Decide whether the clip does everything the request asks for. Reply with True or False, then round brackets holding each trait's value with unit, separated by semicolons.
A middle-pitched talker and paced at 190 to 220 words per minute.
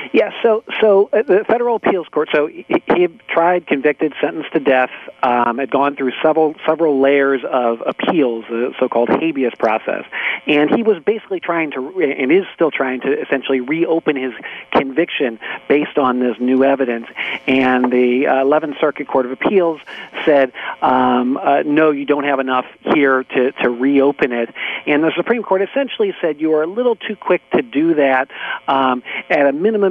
False (145 Hz; 180 wpm)